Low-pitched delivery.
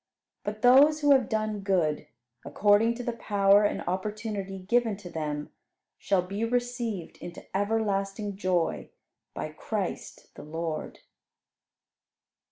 No: high, 205 Hz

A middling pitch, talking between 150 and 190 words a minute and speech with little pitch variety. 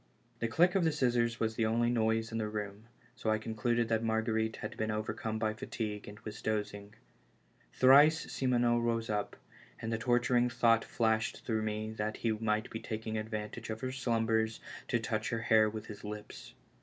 No: low, 110 Hz; average, 185 wpm; narrow, 1.5 semitones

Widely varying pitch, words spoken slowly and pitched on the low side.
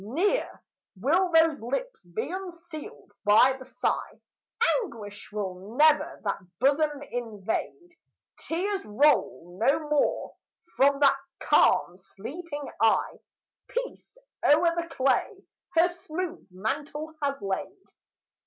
No: wide, 7.5 semitones; slow, 105 wpm; very high, 290 Hz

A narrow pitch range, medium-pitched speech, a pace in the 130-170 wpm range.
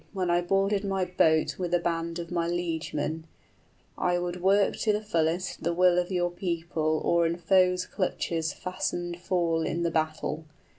No: narrow, 1.6 semitones; medium, 175 Hz; average, 180 wpm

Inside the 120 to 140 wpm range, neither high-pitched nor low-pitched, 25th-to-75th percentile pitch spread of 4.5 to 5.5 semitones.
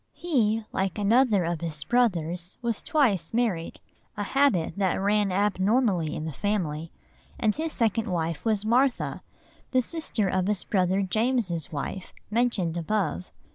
No: slow, 135 wpm; high, 205 Hz; average, 5.0 semitones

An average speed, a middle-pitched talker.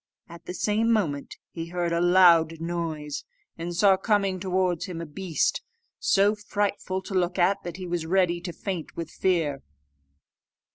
Yes: average, 160 wpm; medium, 175 Hz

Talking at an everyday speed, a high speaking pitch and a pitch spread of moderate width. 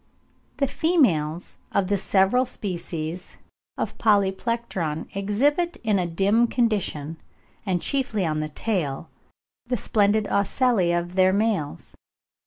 No: slow, 115 wpm; high, 195 Hz; average, 5.0 semitones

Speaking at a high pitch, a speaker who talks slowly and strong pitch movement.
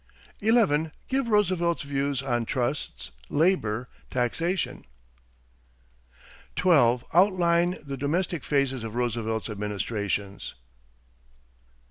No: medium, 140 Hz; slow, 80 wpm; wide, 6.6 semitones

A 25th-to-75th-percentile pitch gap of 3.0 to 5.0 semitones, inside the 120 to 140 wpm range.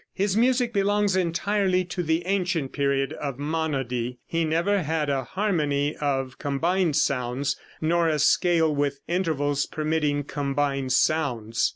Yes: average, 4.2 semitones; slow, 135 wpm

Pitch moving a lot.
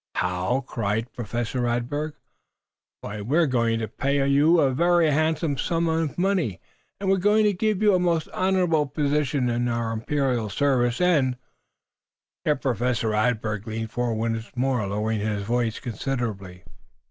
Yes: wide, 5.7 semitones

